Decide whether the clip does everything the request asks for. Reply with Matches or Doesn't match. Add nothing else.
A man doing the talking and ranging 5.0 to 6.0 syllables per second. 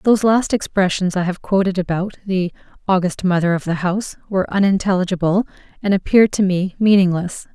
Doesn't match